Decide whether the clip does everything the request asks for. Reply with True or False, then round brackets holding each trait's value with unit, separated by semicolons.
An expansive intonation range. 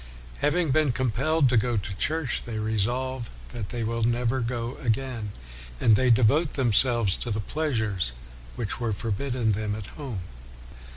False (3.2 semitones)